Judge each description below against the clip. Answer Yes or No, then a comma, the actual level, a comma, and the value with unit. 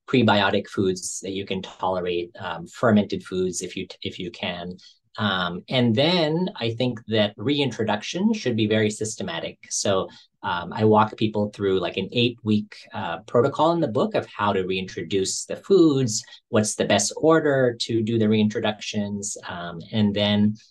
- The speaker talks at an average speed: Yes, average, 165 wpm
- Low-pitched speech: Yes, low, 105 Hz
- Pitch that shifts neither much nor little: Yes, average, 3.6 semitones